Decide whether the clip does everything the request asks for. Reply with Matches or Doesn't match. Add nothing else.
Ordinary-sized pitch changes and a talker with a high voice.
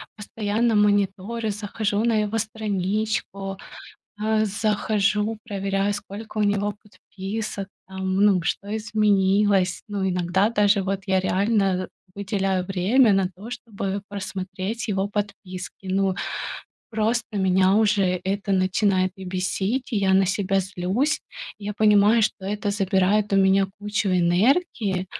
Doesn't match